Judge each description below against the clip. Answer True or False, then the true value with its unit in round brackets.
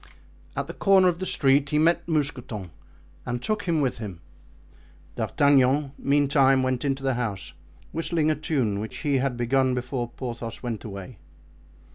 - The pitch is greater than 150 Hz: False (135 Hz)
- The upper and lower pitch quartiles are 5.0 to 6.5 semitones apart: False (3.5 semitones)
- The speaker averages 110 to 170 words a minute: True (155 wpm)